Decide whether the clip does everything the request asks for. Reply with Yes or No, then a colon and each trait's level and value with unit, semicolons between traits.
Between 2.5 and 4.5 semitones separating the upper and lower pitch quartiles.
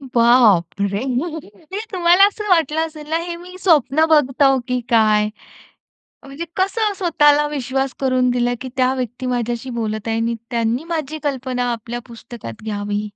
No: average, 5.0 semitones